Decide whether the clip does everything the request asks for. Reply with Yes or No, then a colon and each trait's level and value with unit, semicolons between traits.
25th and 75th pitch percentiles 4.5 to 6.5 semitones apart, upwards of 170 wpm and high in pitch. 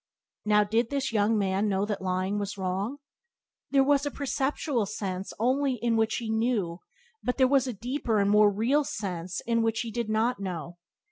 No: average, 4.0 semitones; average, 190 wpm; high, 220 Hz